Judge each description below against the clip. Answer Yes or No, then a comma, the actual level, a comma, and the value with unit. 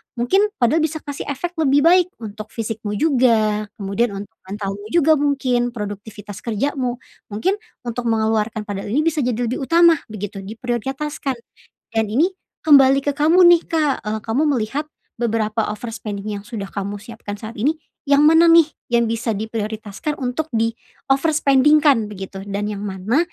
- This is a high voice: Yes, high, 235 Hz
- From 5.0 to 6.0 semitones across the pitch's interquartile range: Yes, wide, 5.6 semitones